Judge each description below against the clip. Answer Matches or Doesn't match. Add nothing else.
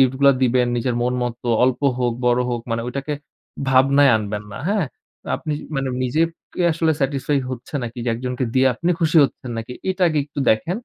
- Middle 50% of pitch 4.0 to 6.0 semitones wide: Doesn't match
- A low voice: Matches